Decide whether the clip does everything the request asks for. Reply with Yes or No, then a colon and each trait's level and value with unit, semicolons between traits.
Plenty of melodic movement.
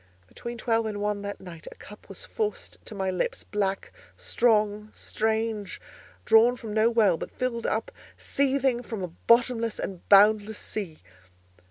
No: narrow, 2.4 semitones